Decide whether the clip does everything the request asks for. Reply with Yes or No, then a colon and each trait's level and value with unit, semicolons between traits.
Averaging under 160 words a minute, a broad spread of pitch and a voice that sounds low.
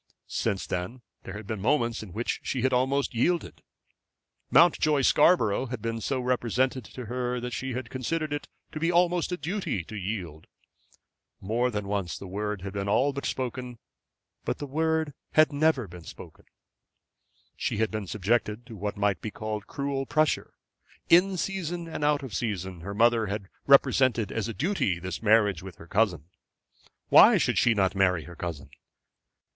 No: average, 175 wpm; wide, 5.7 semitones; low, 115 Hz